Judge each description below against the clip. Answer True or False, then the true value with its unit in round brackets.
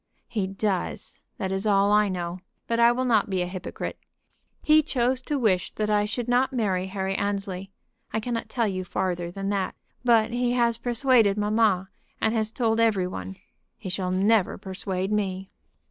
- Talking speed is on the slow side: False (175 wpm)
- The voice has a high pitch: True (205 Hz)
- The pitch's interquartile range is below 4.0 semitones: True (3.5 semitones)